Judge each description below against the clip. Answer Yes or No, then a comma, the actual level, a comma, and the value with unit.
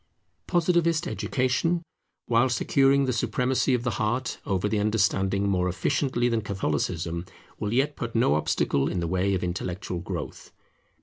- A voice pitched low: Yes, low, 110 Hz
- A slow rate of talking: No, average, 145 wpm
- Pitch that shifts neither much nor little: No, wide, 5.7 semitones